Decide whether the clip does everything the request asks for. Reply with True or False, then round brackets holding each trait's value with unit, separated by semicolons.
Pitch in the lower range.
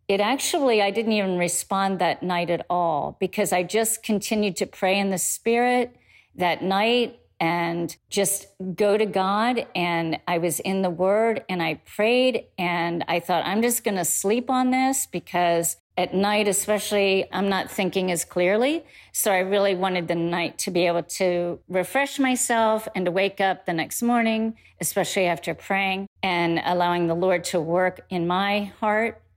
False (190 Hz)